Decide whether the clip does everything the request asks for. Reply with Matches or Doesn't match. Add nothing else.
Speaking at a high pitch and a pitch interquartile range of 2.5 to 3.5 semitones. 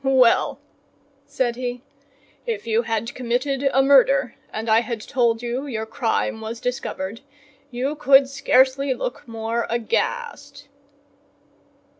Matches